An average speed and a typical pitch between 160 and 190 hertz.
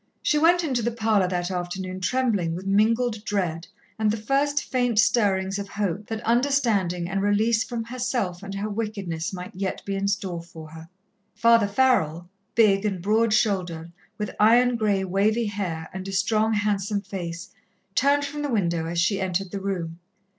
No: average, 175 wpm; high, 200 Hz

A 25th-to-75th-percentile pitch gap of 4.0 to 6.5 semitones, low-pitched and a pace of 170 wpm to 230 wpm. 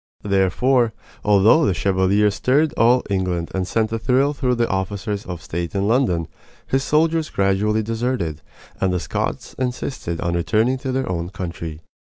No: wide, 5.5 semitones; low, 105 Hz; average, 160 wpm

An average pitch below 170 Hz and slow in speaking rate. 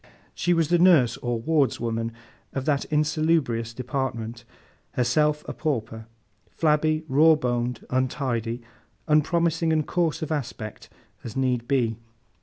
Yes: low, 135 Hz; slow, 105 wpm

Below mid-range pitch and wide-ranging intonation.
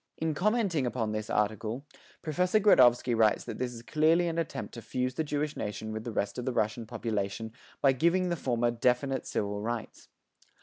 Yes: low, 125 Hz; wide, 5.7 semitones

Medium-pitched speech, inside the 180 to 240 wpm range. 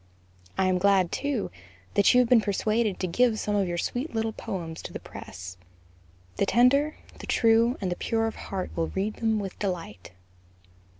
No: high, 205 Hz; average, 185 wpm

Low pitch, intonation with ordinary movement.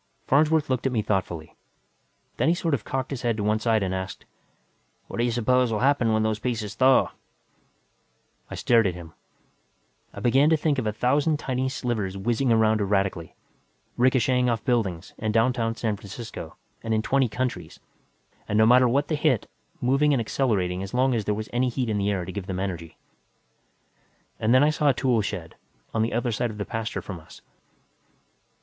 Yes: low, 115 Hz; average, 3.7 semitones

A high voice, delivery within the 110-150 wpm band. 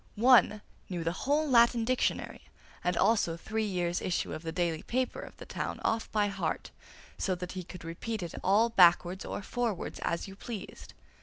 No: high, 195 Hz; average, 180 wpm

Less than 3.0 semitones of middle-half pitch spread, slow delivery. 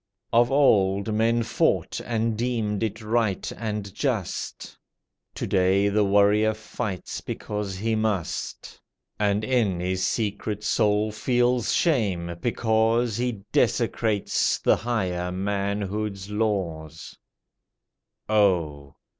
Yes: narrow, 2.5 semitones; slow, 105 wpm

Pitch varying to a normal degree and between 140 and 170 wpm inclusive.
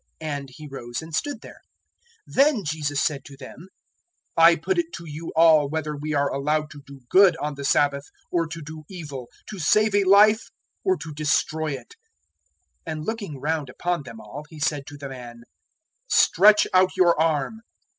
No: average, 3.8 semitones; average, 185 wpm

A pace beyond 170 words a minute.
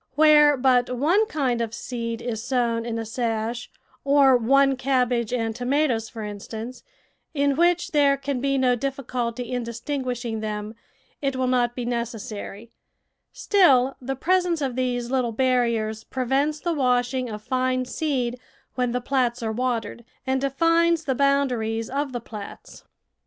No: average, 150 wpm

